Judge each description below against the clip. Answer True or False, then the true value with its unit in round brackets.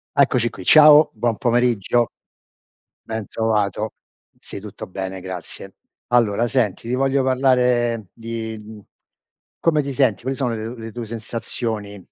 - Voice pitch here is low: True (115 Hz)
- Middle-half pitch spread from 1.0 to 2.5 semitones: False (2.9 semitones)